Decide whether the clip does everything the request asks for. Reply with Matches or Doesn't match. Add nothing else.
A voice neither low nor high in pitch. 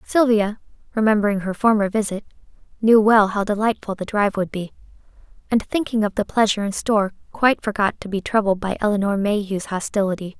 Doesn't match